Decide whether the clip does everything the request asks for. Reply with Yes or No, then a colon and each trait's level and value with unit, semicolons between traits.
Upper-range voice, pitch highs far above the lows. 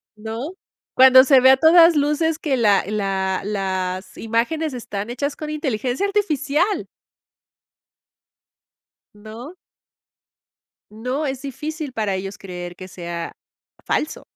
Yes: very high, 250 Hz; wide, 7.1 semitones